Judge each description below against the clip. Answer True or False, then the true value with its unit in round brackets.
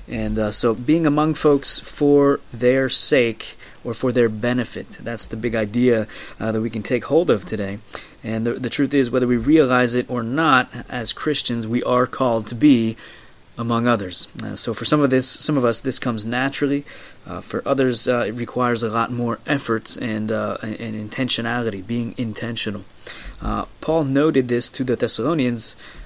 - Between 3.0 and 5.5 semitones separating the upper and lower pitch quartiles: False (2.6 semitones)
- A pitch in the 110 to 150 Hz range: True (120 Hz)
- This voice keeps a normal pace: True (180 wpm)